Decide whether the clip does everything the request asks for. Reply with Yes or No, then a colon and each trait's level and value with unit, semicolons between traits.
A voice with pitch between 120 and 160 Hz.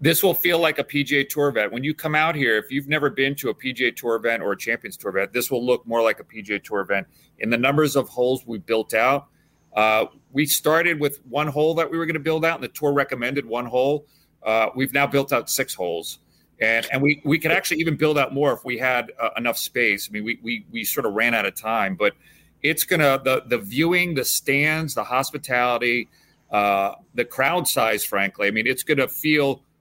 Yes: low, 135 Hz